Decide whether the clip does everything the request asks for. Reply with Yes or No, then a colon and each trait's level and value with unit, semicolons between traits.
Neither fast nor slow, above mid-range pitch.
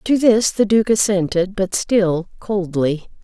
Yes: average, 150 wpm; high, 195 Hz